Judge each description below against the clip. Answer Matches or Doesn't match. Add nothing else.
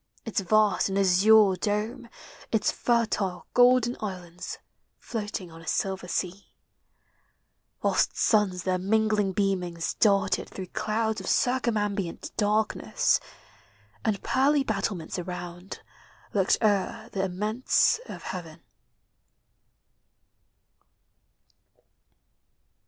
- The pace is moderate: Doesn't match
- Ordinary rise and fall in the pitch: Matches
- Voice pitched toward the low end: Doesn't match